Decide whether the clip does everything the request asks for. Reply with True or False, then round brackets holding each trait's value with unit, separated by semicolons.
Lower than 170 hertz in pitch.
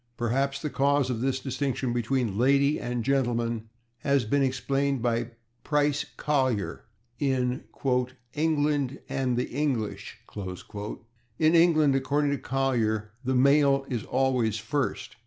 True (135 Hz)